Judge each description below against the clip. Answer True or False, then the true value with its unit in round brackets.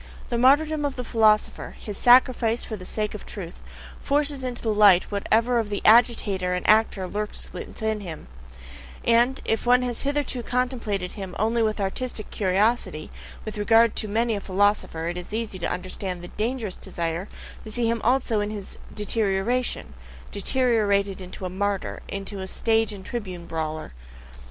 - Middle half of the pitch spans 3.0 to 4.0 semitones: True (3.6 semitones)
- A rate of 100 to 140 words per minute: False (165 wpm)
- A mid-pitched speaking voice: False (215 Hz)